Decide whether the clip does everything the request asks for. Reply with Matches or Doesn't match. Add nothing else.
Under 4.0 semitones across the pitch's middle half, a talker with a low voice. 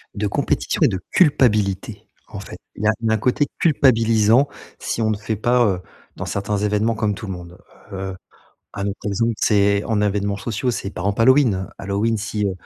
Matches